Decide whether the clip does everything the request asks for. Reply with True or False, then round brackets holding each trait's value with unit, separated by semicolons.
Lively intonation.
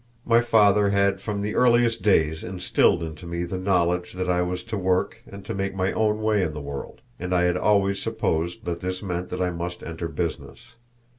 False (2.5 semitones)